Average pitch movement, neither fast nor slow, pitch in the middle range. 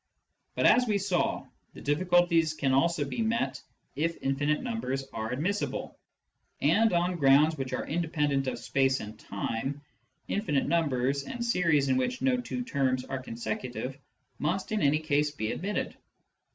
Yes: average, 5.0 semitones; average, 150 wpm; medium, 150 Hz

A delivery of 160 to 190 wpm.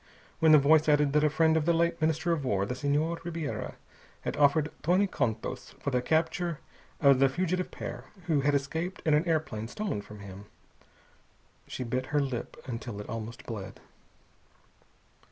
Yes: average, 170 wpm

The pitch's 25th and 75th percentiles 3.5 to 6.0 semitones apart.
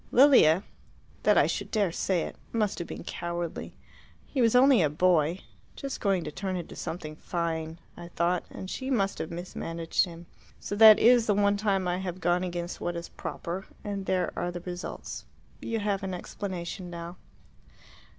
No: average, 2.9 semitones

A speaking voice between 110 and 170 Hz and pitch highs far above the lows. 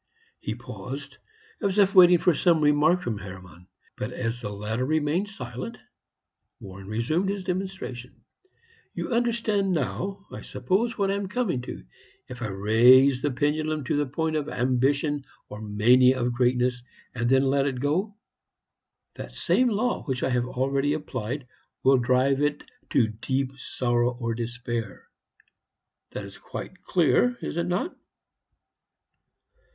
Yes: low, 135 Hz; wide, 6.4 semitones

